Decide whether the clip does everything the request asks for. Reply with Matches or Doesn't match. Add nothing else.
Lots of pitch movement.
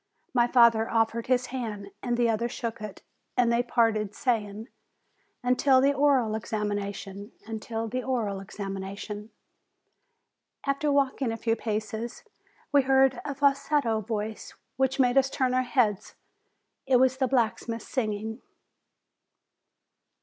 Doesn't match